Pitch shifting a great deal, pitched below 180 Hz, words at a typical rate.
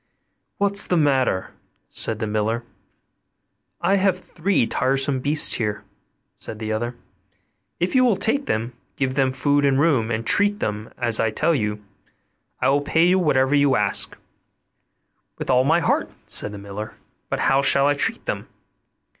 Yes: wide, 6.5 semitones; low, 135 Hz; average, 165 wpm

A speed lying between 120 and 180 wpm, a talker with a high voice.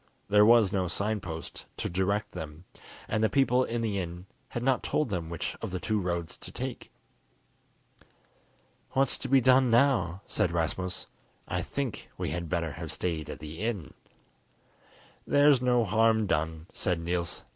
No: average, 165 wpm; very low, 95 Hz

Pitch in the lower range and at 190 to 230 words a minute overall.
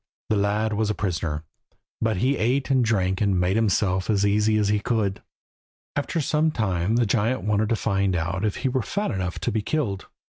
Yes: low, 105 Hz; average, 200 wpm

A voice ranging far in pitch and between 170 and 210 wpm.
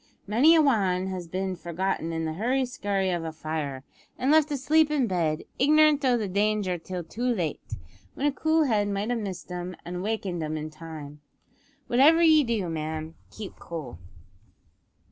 Yes: wide, 7.4 semitones; average, 175 wpm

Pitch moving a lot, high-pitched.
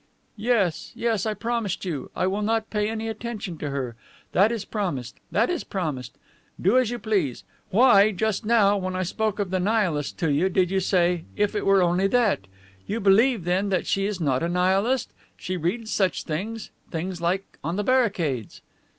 No: average, 3.9 semitones; high, 195 Hz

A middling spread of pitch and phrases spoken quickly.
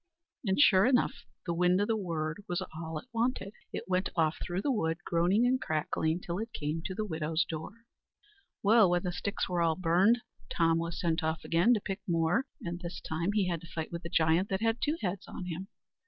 Yes: average, 3.7 semitones; fast, 220 wpm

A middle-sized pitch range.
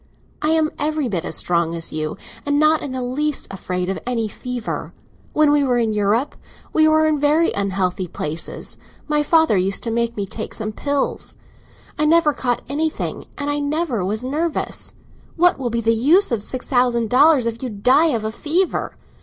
No: wide, 5.9 semitones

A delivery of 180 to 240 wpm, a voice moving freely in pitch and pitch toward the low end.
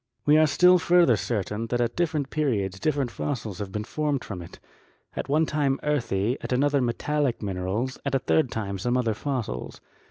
Yes: average, 185 wpm; wide, 5.8 semitones; low, 125 Hz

